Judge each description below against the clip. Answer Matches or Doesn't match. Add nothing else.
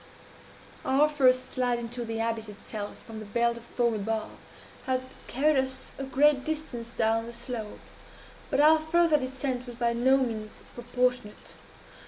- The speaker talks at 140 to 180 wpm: Matches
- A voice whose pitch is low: Doesn't match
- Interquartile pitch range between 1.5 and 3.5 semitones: Matches